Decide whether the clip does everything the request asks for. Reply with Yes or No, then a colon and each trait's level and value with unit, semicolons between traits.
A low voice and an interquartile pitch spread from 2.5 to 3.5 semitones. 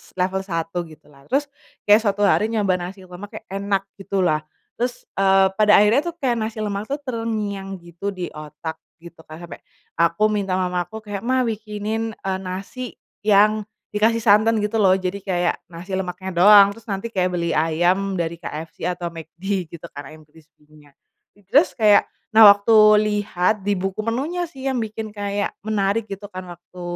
No: high, 195 Hz; average, 3.2 semitones